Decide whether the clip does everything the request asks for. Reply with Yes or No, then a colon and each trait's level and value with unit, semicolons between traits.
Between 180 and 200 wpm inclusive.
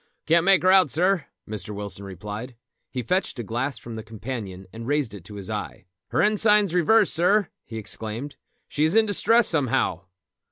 Yes: average, 185 wpm